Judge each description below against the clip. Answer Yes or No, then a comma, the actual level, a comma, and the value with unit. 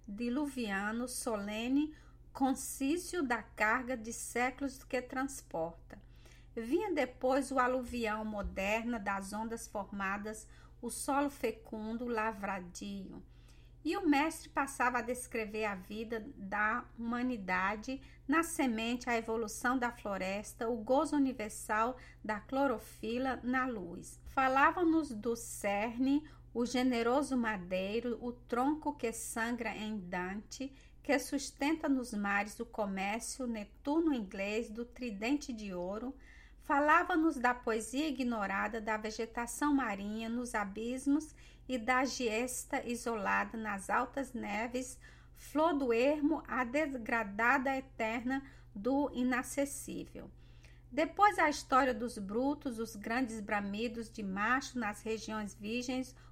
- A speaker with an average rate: No, slow, 110 wpm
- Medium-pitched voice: No, high, 240 Hz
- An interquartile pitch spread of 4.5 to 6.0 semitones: No, average, 3.8 semitones